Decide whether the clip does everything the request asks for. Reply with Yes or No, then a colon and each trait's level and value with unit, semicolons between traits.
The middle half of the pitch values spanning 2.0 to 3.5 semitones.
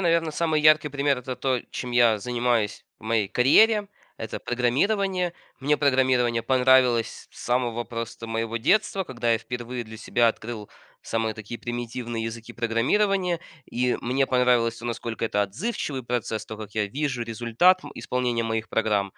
Yes: average, 2.9 semitones